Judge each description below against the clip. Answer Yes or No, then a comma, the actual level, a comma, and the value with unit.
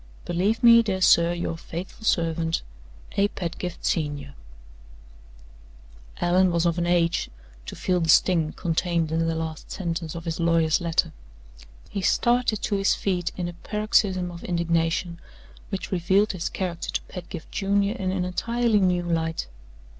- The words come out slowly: No, average, 150 wpm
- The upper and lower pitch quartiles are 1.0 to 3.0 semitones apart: Yes, narrow, 2.5 semitones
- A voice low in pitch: No, medium, 175 Hz